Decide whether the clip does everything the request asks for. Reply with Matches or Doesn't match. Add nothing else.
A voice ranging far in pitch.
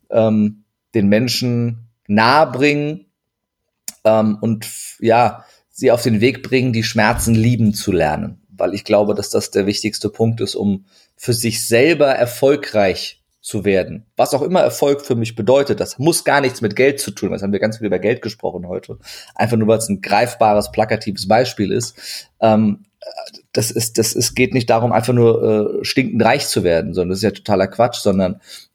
Doesn't match